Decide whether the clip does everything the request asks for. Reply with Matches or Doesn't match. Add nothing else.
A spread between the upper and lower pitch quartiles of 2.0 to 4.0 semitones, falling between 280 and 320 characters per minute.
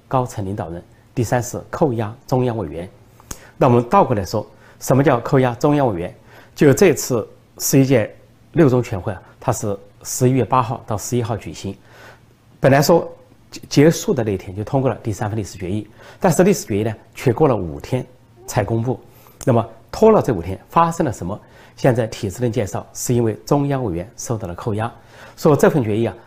Matches